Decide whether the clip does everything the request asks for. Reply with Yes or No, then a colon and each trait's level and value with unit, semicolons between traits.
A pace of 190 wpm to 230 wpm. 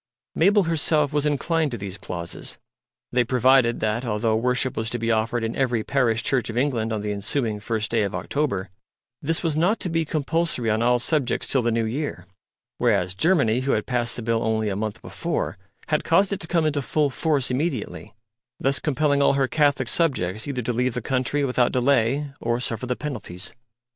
Yes: average, 200 wpm